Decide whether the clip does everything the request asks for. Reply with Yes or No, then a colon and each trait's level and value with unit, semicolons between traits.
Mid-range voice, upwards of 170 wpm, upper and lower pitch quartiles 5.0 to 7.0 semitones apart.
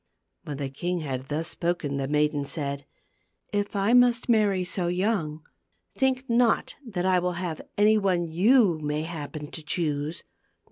No: medium, 175 Hz; average, 160 wpm; wide, 5.4 semitones